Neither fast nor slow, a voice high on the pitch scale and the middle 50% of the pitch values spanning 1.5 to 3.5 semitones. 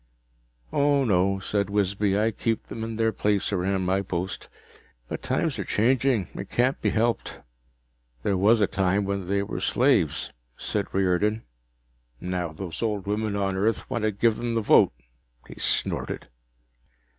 No: average, 155 wpm; low, 100 Hz; average, 2.7 semitones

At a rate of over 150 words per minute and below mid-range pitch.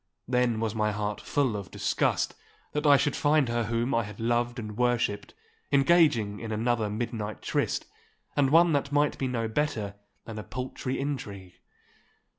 Yes: average, 165 wpm; low, 120 Hz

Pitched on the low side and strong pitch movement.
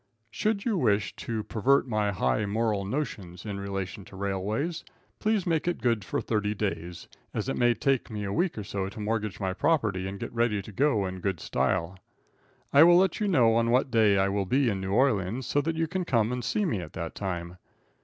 Yes: low, 110 Hz; wide, 5.8 semitones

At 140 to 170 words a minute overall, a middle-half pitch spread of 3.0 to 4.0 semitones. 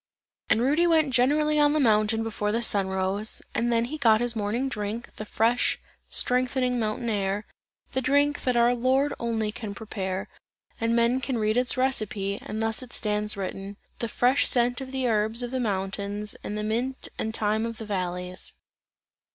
No: average, 185 wpm; average, 3.3 semitones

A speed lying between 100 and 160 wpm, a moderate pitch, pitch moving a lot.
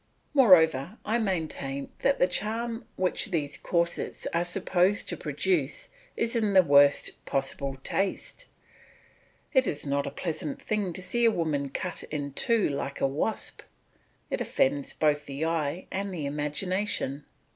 Yes: average, 145 wpm; medium, 170 Hz; wide, 6.0 semitones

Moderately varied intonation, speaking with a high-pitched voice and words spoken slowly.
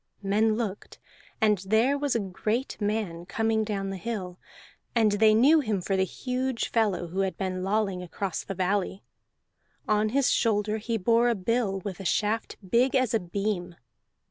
No: average, 3.0 semitones; high, 210 Hz; average, 170 wpm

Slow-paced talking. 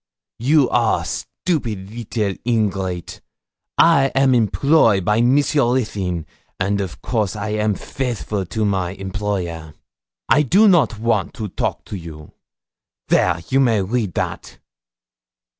Yes: slow, 125 wpm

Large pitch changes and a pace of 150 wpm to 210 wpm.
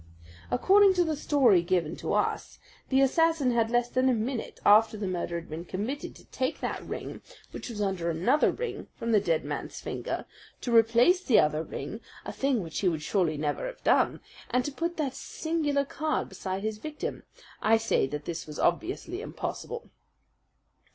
Yes: wide, 8.3 semitones; average, 185 wpm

